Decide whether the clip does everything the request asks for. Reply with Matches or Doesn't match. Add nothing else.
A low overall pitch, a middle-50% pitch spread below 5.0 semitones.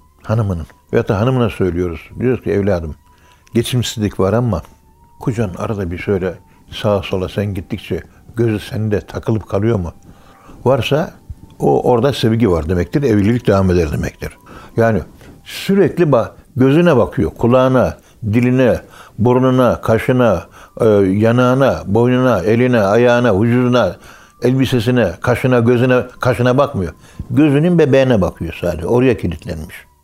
Doesn't match